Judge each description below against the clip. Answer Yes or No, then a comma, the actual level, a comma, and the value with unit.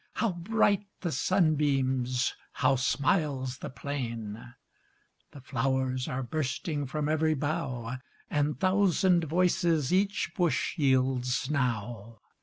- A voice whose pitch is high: No, medium, 140 Hz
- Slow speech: Yes, slow, 105 wpm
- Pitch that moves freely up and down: No, average, 4.4 semitones